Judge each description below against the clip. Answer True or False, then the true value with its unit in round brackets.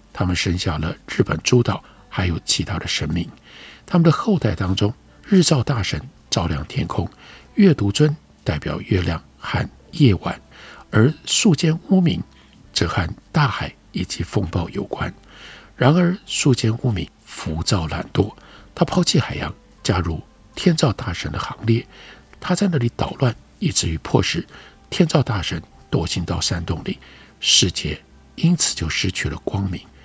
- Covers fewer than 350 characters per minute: True (220 characters per minute)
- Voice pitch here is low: True (125 Hz)